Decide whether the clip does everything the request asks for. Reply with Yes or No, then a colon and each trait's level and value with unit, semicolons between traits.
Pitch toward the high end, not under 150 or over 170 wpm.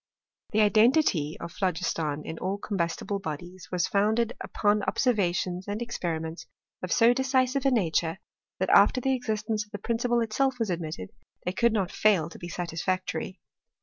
Yes: high, 205 Hz; average, 160 wpm